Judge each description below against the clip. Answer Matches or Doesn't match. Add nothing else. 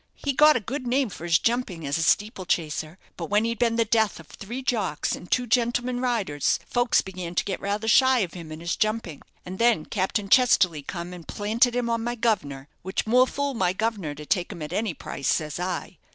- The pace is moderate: Doesn't match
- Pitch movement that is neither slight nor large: Doesn't match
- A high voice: Matches